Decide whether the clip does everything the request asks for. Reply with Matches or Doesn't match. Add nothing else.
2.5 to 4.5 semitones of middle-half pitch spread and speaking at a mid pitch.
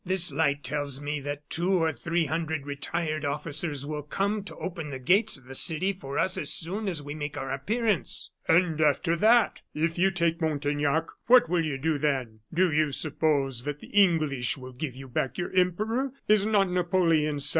Matches